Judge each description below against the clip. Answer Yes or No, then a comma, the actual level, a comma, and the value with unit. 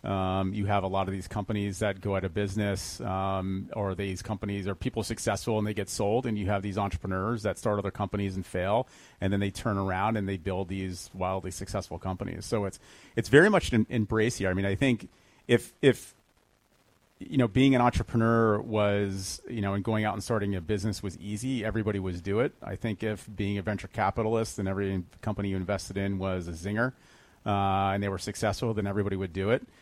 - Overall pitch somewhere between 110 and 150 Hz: No, low, 100 Hz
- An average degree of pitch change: No, narrow, 2.1 semitones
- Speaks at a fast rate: Yes, fast, 215 wpm